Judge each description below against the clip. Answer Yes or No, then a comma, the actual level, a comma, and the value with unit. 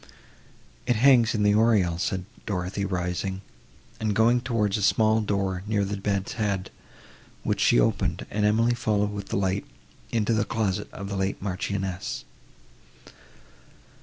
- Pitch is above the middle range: No, low, 100 Hz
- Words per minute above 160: No, average, 145 wpm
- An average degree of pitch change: No, narrow, 2.3 semitones